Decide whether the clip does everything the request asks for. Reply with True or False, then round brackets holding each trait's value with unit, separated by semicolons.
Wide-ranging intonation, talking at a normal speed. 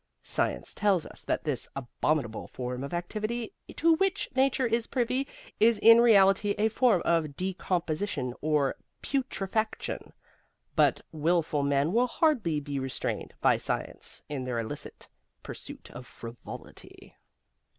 False (8.4 semitones; 130 wpm)